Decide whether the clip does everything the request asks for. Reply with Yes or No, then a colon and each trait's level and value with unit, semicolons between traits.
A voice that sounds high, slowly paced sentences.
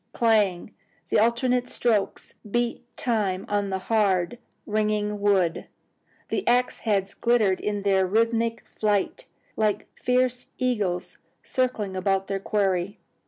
Yes: high, 210 Hz; slow, 115 wpm